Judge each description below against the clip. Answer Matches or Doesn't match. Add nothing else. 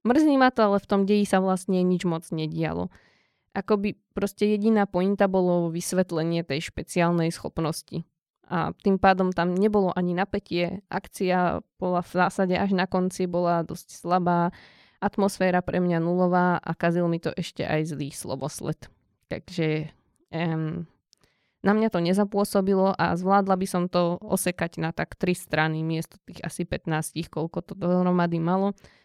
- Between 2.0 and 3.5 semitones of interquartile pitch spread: Matches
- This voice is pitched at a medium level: Matches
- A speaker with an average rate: Matches